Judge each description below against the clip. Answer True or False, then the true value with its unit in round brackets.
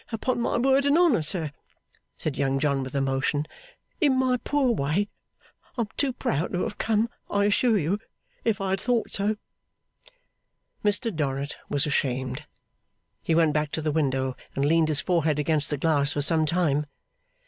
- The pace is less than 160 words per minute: False (170 wpm)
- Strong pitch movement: True (7.0 semitones)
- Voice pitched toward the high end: False (160 Hz)